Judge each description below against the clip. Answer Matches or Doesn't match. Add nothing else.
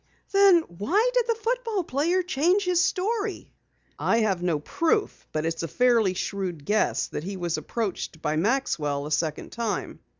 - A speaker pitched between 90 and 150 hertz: Doesn't match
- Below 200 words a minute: Matches